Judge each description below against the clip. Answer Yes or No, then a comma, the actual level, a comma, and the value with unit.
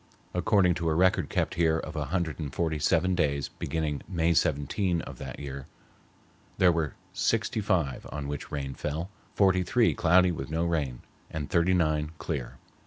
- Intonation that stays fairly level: No, average, 3.2 semitones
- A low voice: Yes, very low, 80 Hz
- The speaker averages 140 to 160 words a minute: No, average, 175 wpm